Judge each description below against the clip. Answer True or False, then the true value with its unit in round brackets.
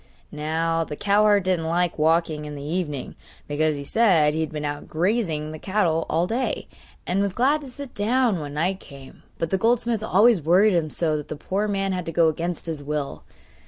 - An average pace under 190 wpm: False (205 wpm)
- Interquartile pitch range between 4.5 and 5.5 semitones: True (4.9 semitones)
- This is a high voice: False (170 Hz)